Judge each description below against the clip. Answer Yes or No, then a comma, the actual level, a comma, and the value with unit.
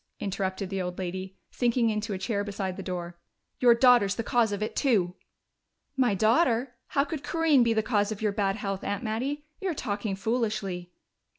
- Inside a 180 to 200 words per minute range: Yes, average, 185 wpm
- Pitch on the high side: Yes, high, 215 Hz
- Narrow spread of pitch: No, average, 3.8 semitones